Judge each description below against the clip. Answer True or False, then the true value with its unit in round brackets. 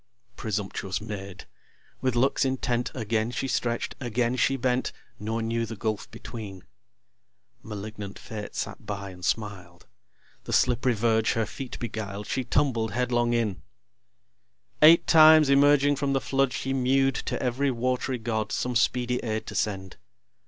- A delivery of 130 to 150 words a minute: True (145 wpm)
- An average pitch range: True (3.3 semitones)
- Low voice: True (120 Hz)